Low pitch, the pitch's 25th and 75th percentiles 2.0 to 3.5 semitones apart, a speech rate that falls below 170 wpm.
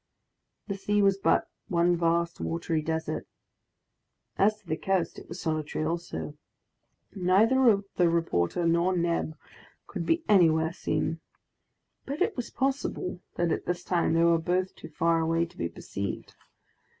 No: medium, 170 Hz; average, 2.8 semitones; average, 150 wpm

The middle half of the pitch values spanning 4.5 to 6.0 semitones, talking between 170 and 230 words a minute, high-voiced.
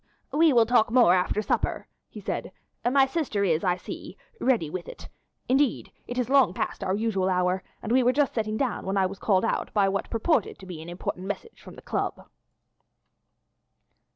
Yes: average, 5.2 semitones; average, 195 wpm; high, 215 Hz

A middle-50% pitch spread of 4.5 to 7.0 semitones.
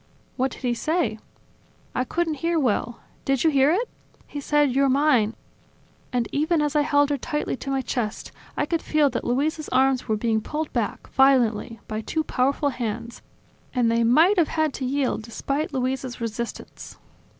No: average, 3.9 semitones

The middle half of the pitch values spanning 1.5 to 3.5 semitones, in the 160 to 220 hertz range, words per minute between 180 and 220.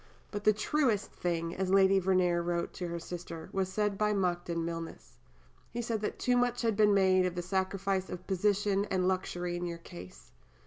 Yes: average, 2.7 semitones; high, 190 Hz; average, 190 wpm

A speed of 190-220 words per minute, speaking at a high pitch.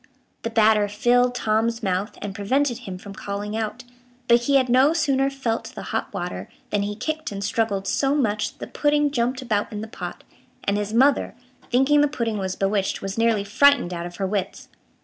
Yes: average, 200 wpm; high, 225 Hz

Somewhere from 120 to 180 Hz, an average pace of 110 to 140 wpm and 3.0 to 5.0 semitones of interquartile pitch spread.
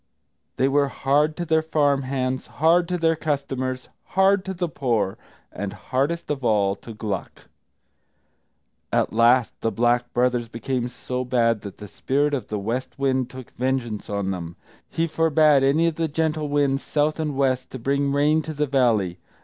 No: low, 135 Hz; average, 175 wpm; average, 4.1 semitones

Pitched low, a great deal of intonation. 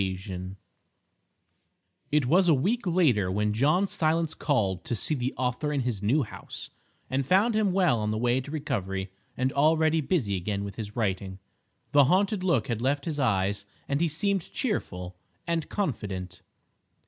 Yes: low, 130 Hz; wide, 8.0 semitones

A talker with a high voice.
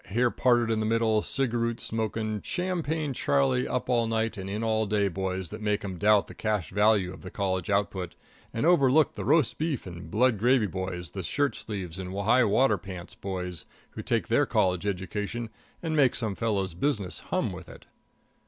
No: low, 110 Hz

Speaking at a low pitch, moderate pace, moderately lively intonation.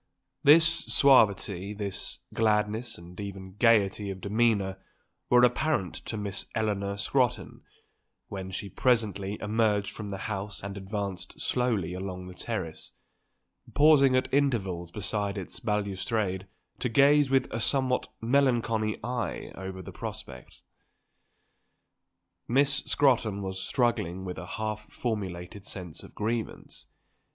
No: low, 105 Hz; slow, 120 wpm; average, 3.7 semitones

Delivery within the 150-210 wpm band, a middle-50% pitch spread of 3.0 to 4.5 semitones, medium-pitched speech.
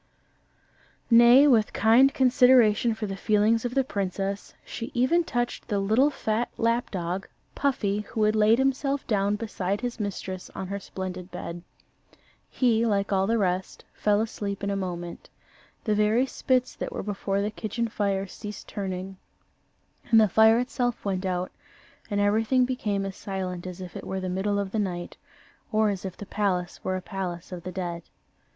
No: average, 175 wpm; average, 3.3 semitones; high, 205 Hz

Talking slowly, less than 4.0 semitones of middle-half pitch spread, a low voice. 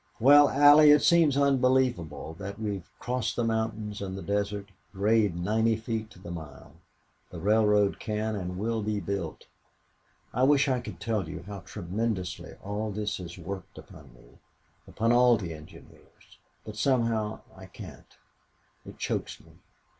No: average, 155 wpm; average, 3.1 semitones; low, 105 Hz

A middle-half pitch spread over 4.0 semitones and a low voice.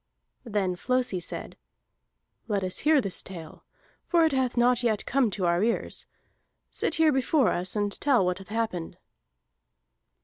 No: wide, 5.5 semitones; high, 220 Hz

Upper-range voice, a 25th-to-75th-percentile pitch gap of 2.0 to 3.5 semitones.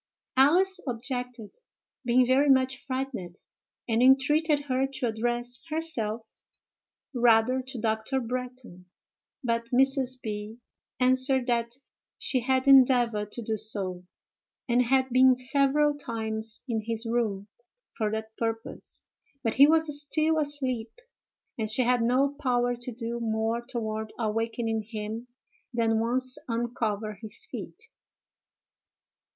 Yes: high, 240 Hz; average, 2.8 semitones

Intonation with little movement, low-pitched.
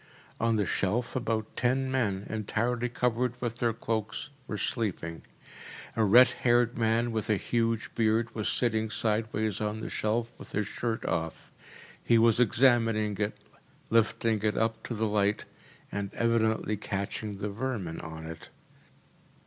Yes: narrow, 2.0 semitones; low, 110 Hz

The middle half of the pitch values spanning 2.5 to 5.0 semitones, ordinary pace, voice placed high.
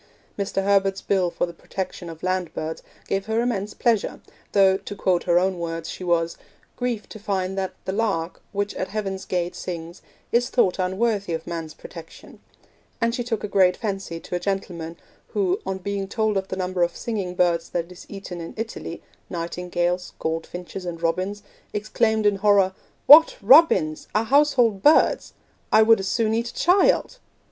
Yes: average, 3.5 semitones; average, 175 wpm; high, 195 Hz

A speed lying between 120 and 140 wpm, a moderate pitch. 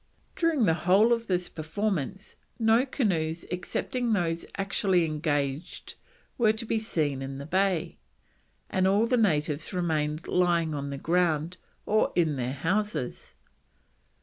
Yes: slow, 135 wpm; medium, 175 Hz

